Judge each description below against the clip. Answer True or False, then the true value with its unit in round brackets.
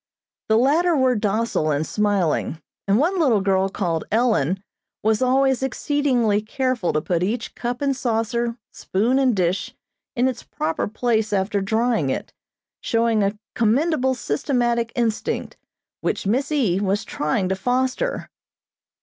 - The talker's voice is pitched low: False (225 Hz)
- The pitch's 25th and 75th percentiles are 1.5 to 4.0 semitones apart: False (4.5 semitones)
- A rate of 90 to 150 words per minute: True (140 wpm)